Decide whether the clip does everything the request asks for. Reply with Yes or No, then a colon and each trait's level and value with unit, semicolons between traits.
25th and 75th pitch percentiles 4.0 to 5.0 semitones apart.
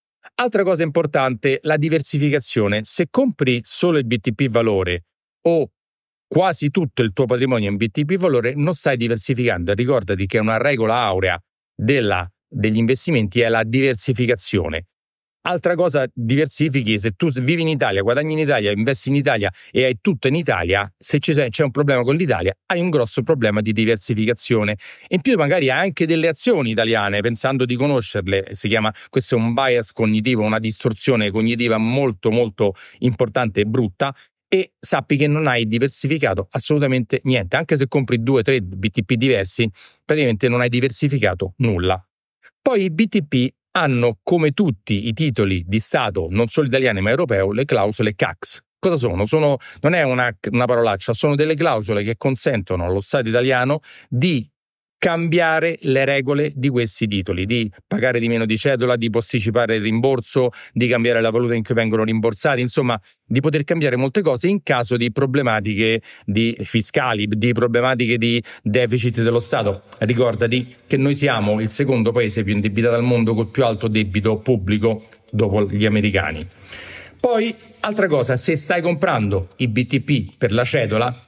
Yes: average, 4.6 semitones